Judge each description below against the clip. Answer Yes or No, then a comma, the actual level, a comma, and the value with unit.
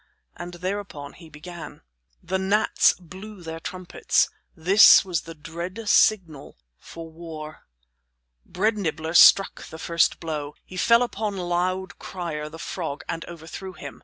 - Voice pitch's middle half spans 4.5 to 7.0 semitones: No, average, 2.8 semitones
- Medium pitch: Yes, medium, 175 Hz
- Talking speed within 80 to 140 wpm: Yes, slow, 135 wpm